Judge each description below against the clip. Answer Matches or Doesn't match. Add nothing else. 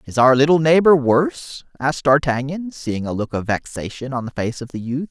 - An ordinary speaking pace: Doesn't match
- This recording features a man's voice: Matches